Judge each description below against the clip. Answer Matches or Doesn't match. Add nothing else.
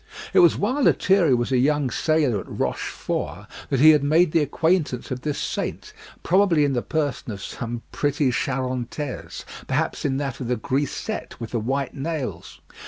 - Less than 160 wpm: Doesn't match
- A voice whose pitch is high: Doesn't match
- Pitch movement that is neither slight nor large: Matches